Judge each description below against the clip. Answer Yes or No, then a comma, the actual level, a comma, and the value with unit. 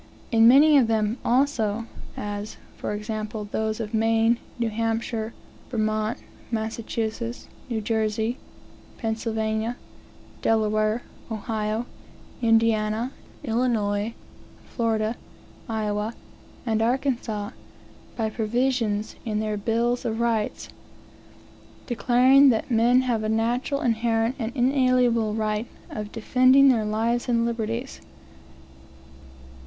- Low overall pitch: No, high, 225 Hz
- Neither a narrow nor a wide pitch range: No, narrow, 1.8 semitones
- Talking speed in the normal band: No, slow, 100 wpm